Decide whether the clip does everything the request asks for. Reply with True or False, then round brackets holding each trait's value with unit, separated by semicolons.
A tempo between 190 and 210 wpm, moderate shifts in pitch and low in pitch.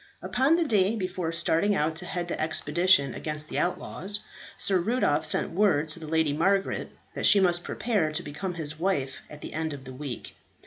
False (195 wpm; 4.2 semitones; 170 Hz)